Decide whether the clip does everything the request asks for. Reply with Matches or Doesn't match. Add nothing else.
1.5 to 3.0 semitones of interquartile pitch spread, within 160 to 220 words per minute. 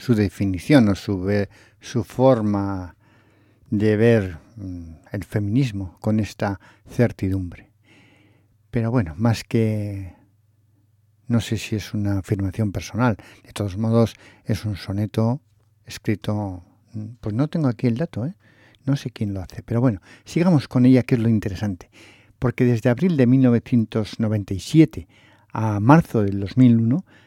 Doesn't match